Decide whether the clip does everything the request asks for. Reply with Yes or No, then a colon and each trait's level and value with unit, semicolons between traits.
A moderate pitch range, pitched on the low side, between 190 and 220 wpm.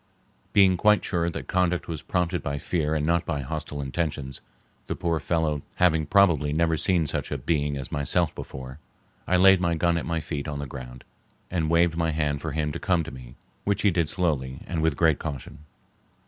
Yes: average, 3.0 semitones; very low, 80 Hz; fast, 205 wpm